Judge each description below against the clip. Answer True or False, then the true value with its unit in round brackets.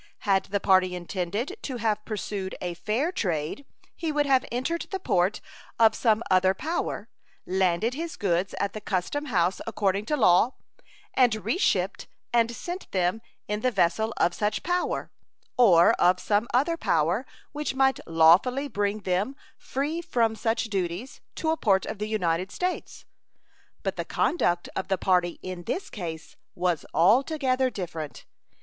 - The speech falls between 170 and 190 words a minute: False (155 wpm)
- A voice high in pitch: True (210 Hz)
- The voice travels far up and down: True (6.1 semitones)